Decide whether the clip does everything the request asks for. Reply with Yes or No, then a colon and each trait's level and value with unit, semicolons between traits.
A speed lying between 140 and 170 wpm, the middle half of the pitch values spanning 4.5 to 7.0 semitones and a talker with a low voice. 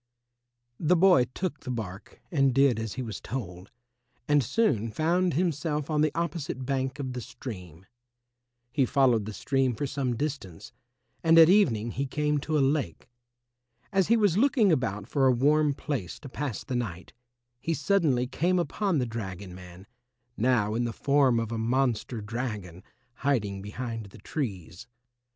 Yes: average, 165 wpm; average, 5.3 semitones; low, 130 Hz